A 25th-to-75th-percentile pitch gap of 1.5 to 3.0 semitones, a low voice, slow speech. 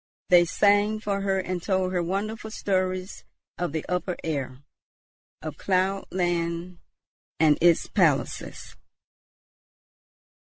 No: narrow, 2.4 semitones; medium, 185 Hz; slow, 110 wpm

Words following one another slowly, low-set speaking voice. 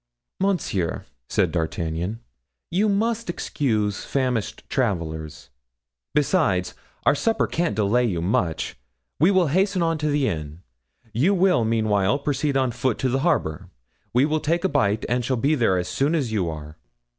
No: average, 155 wpm; low, 125 Hz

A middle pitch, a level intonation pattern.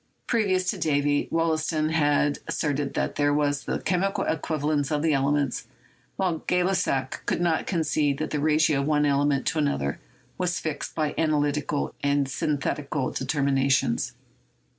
Yes: medium, 150 Hz; narrow, 2.1 semitones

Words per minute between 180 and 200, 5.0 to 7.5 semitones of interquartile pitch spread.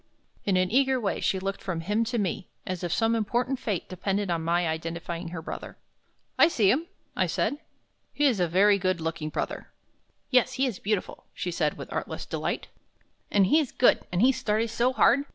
Yes: average, 195 wpm; wide, 5.5 semitones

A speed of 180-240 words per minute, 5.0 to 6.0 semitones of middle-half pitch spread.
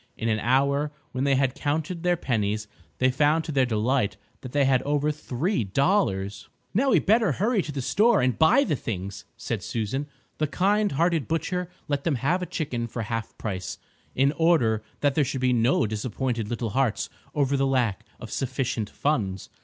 Yes: average, 190 wpm; wide, 5.4 semitones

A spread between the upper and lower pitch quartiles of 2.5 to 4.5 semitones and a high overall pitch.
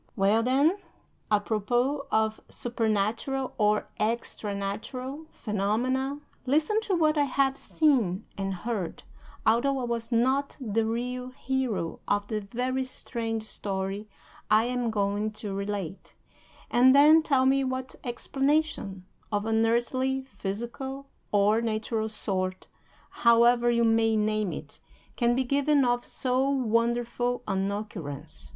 Yes: average, 3.9 semitones; high, 235 Hz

